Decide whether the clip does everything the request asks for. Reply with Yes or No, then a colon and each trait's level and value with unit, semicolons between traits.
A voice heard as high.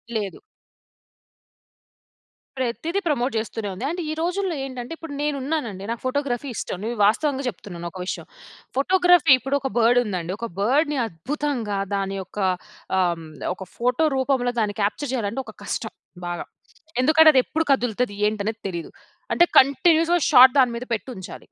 Yes: very high, 250 Hz